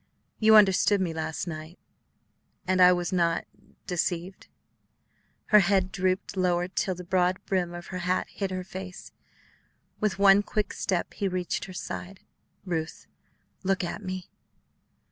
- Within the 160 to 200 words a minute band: No, average, 145 wpm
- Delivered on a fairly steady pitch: Yes, narrow, 1.6 semitones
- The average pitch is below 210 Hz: Yes, medium, 185 Hz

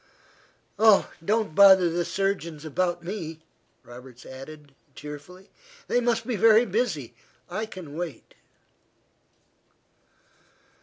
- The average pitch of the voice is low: No, medium, 175 Hz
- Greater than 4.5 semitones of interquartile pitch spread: Yes, average, 5.3 semitones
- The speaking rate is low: Yes, slow, 100 wpm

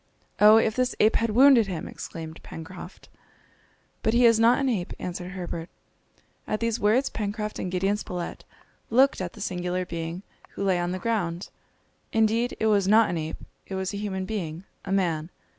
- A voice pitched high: Yes, high, 195 Hz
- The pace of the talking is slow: No, average, 180 wpm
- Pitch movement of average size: Yes, average, 3.9 semitones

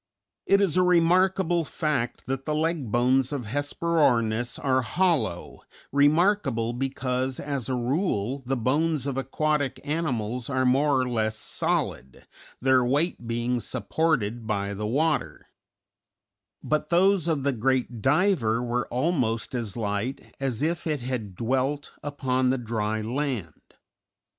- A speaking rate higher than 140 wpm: No, slow, 135 wpm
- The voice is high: No, low, 130 Hz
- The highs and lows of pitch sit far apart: No, average, 4.4 semitones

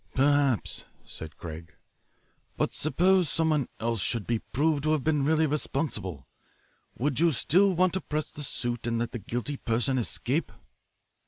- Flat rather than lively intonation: No, average, 4.9 semitones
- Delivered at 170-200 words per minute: No, average, 155 wpm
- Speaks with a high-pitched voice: No, medium, 140 Hz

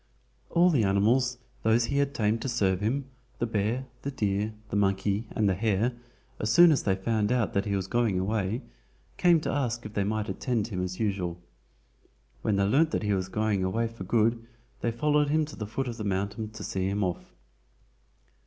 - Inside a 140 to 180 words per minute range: No, fast, 205 wpm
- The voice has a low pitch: Yes, low, 110 Hz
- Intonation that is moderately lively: Yes, average, 3.4 semitones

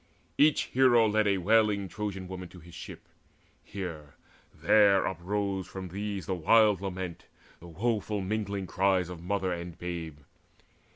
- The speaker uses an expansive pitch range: No, average, 2.8 semitones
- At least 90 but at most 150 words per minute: Yes, average, 140 wpm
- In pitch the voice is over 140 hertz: No, very low, 95 Hz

